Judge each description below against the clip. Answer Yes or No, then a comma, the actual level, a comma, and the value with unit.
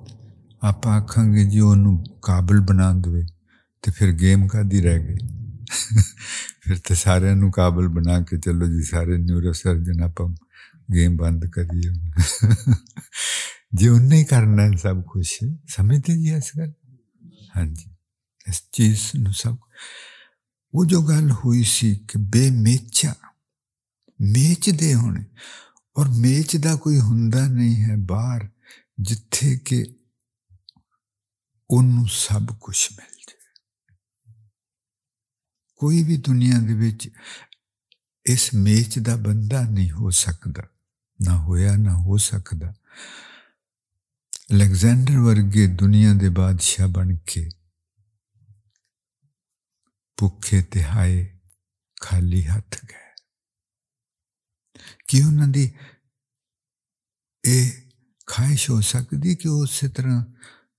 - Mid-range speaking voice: No, low, 105 Hz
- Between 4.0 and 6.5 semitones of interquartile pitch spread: Yes, average, 4.7 semitones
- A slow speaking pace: Yes, slow, 100 wpm